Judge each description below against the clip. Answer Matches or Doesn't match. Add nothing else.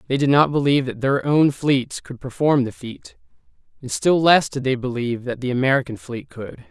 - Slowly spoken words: Doesn't match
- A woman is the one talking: Doesn't match